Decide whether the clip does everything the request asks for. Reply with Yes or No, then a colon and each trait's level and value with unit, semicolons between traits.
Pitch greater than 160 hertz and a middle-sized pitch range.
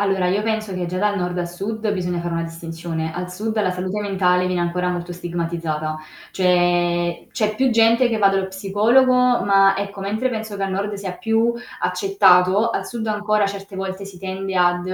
Yes: high, 190 Hz; average, 3.0 semitones